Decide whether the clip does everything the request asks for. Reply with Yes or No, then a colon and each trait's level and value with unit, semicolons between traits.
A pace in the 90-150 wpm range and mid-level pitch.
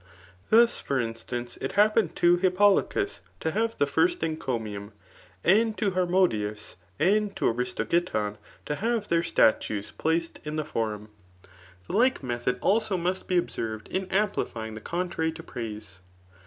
Yes: average, 145 wpm; medium, 165 Hz